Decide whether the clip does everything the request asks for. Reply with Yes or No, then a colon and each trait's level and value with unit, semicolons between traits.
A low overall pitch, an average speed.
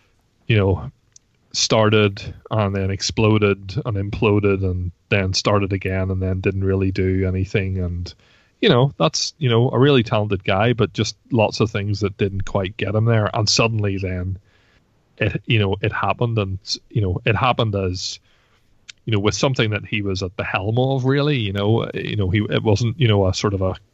Yes: low, 105 Hz; average, 195 wpm